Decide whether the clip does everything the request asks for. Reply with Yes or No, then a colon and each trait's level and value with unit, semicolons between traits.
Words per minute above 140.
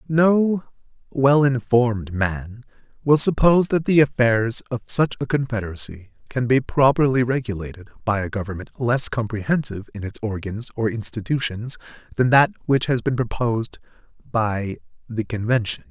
No: slow, 135 wpm